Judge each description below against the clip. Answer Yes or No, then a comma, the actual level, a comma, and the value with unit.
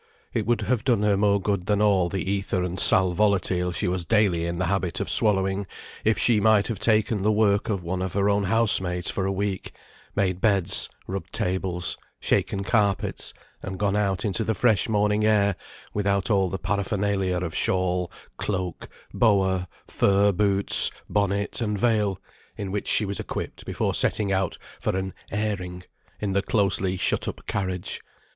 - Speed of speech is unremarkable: Yes, average, 175 wpm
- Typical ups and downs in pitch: No, narrow, 2.0 semitones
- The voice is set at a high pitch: No, low, 100 Hz